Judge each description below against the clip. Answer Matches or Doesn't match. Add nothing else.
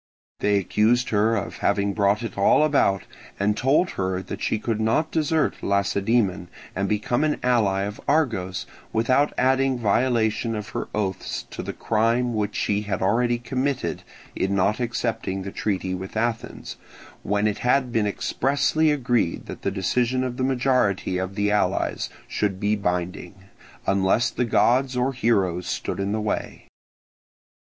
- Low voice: Matches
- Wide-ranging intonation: Doesn't match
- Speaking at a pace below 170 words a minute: Matches